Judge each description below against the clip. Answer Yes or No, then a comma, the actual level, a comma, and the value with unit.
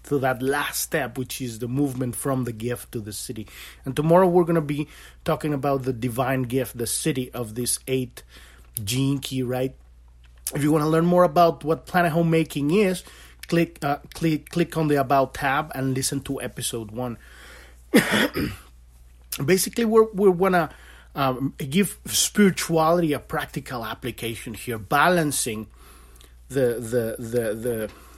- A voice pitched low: Yes, low, 130 Hz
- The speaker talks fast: No, average, 160 wpm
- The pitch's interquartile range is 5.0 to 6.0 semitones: Yes, wide, 5.4 semitones